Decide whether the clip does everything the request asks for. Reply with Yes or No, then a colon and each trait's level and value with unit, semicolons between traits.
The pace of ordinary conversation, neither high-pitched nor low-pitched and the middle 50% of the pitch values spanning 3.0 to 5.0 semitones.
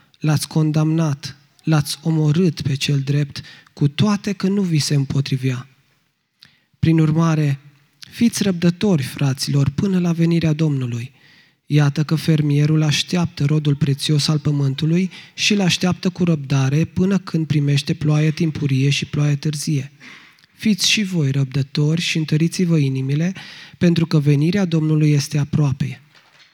No: average, 130 wpm; medium, 155 Hz; narrow, 2.5 semitones